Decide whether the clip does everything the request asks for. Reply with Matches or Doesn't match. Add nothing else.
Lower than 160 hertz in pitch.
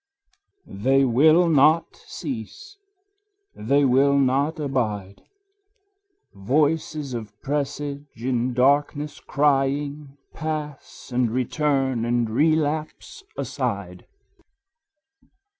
Matches